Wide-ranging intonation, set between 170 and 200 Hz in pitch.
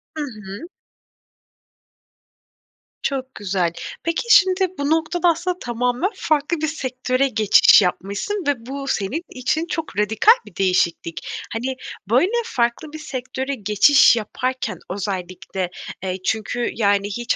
No: wide, 7.1 semitones; very high, 250 Hz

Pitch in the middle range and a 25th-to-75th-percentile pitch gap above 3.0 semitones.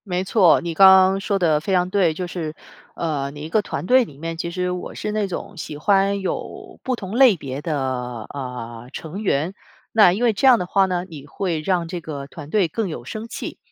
Yes: medium, 180 Hz; average, 4.2 semitones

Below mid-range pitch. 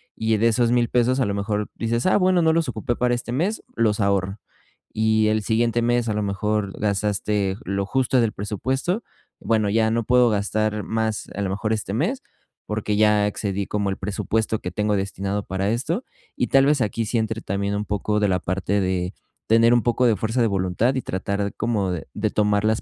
Yes: low, 110 Hz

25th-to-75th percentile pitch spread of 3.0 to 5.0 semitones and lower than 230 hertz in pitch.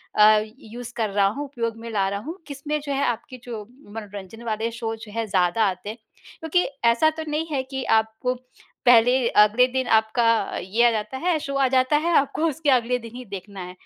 No: average, 4.0 semitones; high, 235 Hz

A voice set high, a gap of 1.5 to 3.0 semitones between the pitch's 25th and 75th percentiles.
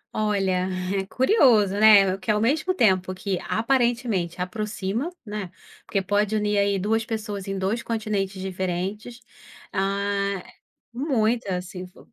Yes: high, 205 Hz; narrow, 2.6 semitones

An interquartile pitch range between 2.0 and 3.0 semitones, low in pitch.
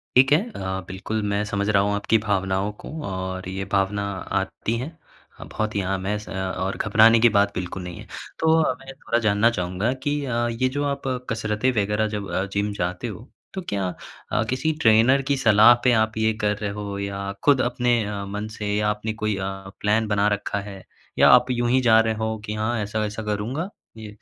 Yes: narrow, 2.5 semitones; low, 105 Hz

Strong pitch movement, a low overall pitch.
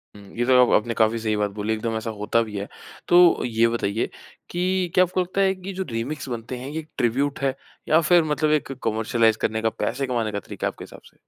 Yes: wide, 5.7 semitones; low, 120 Hz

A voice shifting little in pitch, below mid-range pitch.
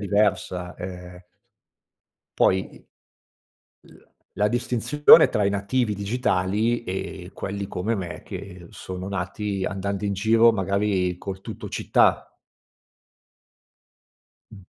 Yes: narrow, 2.2 semitones; low, 100 Hz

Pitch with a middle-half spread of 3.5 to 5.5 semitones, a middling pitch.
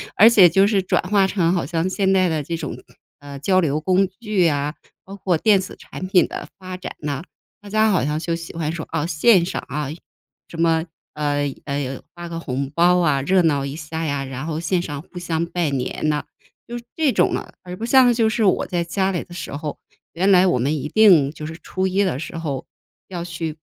Yes: average, 4.0 semitones; medium, 170 Hz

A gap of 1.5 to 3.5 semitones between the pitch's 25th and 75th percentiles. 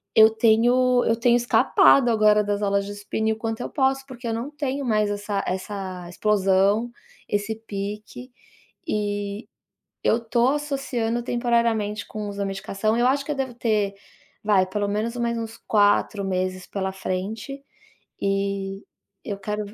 Yes: average, 2.9 semitones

